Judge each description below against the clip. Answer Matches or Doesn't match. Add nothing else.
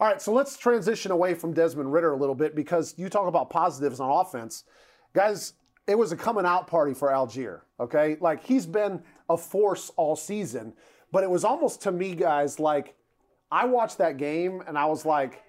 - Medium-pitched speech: Matches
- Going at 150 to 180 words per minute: Doesn't match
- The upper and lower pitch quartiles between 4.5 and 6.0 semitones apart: Matches